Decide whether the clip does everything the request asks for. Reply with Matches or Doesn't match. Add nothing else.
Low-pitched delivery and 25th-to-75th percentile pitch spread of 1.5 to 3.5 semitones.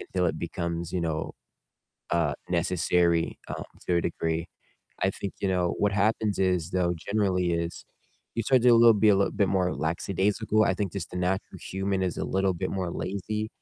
Matches